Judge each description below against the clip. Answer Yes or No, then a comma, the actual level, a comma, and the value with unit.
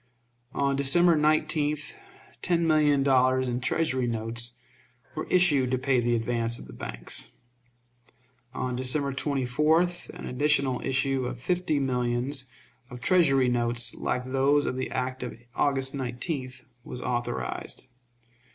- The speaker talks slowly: Yes, slow, 130 wpm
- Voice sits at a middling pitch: No, low, 130 Hz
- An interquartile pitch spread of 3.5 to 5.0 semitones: No, average, 2.9 semitones